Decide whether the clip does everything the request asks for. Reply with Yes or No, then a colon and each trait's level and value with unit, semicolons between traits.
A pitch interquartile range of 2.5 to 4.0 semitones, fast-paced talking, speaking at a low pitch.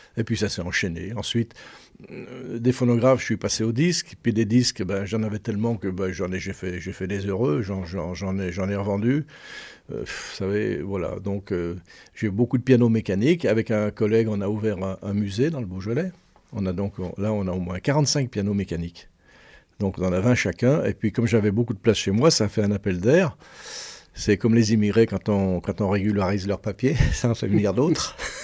Yes: average, 3.5 semitones; fast, 235 wpm; low, 105 Hz